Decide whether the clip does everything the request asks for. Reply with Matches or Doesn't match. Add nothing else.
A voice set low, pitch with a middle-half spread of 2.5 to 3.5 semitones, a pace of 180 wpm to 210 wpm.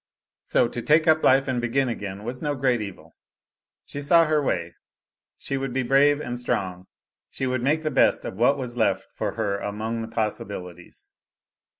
Doesn't match